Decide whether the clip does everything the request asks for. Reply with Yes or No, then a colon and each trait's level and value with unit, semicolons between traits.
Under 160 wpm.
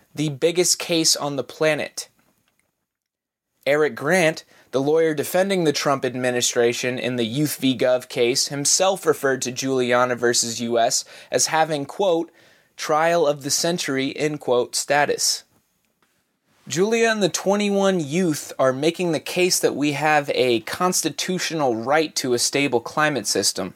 Yes: average, 140 wpm